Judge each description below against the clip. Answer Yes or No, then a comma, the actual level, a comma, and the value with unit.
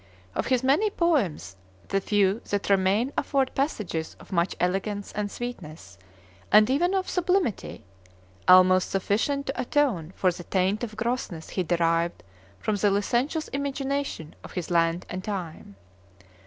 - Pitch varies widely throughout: Yes, wide, 6.9 semitones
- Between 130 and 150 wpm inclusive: Yes, average, 140 wpm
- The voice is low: No, high, 205 Hz